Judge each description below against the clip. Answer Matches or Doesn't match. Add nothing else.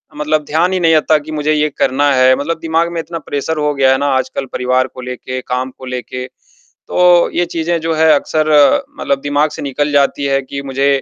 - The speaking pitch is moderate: Matches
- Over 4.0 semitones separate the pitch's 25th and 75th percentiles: Doesn't match